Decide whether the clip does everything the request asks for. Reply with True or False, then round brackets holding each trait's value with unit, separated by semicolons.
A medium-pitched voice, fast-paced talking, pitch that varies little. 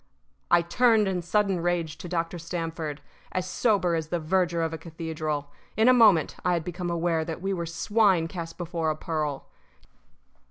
False (170 Hz; 175 wpm; 2.2 semitones)